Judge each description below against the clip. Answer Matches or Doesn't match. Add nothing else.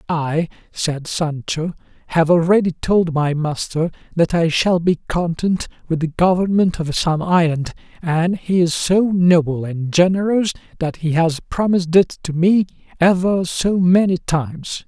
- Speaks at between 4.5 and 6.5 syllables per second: Doesn't match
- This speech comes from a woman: Doesn't match